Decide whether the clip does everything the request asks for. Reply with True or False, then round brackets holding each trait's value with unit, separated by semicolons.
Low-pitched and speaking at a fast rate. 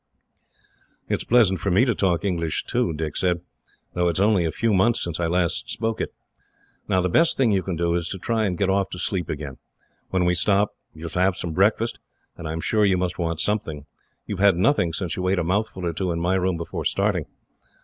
True (90 Hz; 230 wpm)